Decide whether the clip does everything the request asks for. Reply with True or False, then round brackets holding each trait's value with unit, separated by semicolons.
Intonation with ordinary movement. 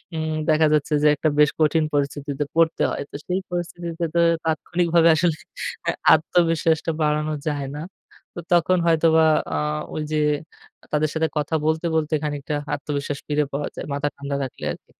False (2.0 semitones)